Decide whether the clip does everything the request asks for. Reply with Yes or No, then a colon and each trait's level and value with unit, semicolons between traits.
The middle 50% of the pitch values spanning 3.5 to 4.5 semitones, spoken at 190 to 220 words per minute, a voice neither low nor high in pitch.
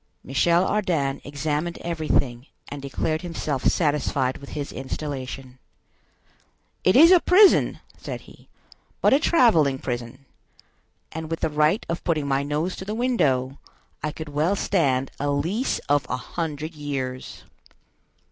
No: average, 3.9 semitones; average, 140 wpm; medium, 150 Hz